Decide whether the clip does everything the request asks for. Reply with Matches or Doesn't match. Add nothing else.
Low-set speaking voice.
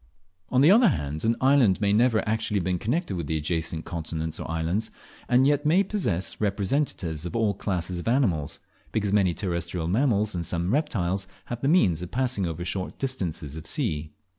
Matches